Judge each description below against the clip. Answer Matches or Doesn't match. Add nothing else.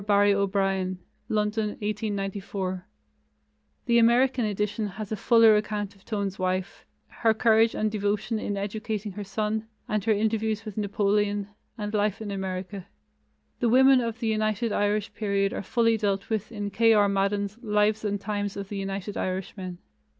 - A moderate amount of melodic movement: Doesn't match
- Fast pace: Doesn't match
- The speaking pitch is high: Matches